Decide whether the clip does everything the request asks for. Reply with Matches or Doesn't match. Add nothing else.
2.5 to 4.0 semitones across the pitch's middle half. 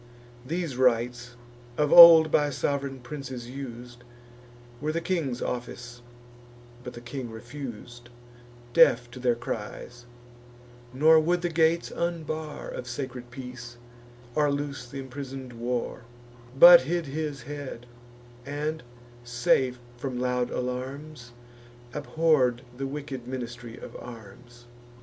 Matches